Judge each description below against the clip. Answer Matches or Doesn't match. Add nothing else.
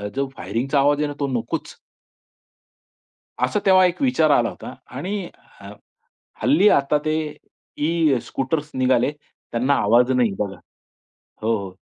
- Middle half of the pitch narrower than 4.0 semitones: Doesn't match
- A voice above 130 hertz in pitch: Matches